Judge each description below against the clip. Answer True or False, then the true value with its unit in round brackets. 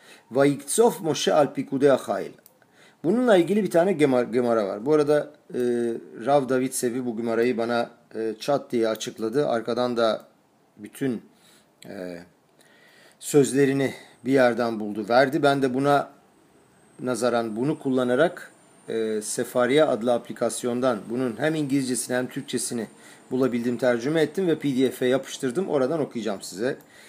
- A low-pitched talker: True (125 Hz)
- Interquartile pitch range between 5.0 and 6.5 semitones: False (3.2 semitones)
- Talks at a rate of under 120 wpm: False (125 wpm)